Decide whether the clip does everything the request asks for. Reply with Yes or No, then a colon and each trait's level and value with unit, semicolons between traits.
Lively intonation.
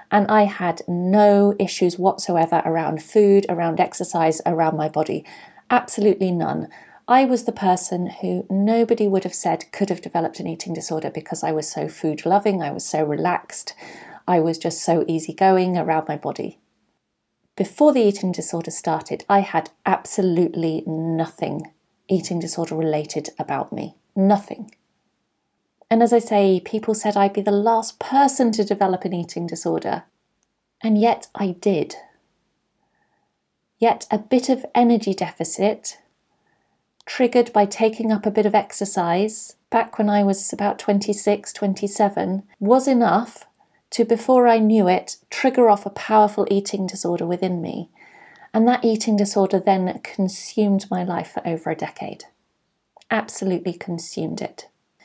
No: average, 4.0 semitones